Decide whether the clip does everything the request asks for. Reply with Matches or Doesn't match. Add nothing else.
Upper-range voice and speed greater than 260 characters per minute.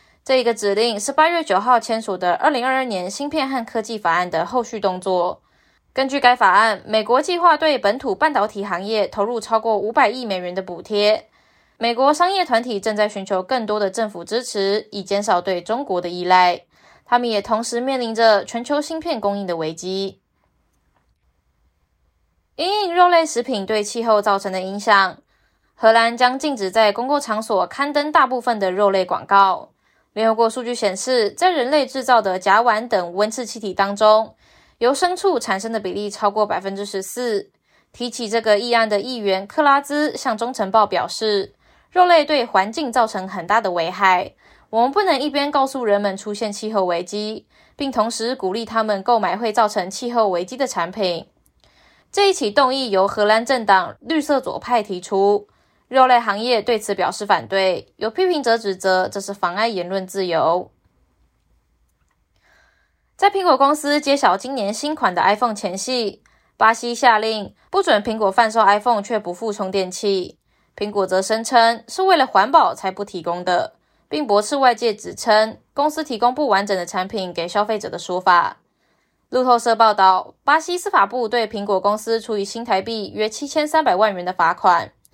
Matches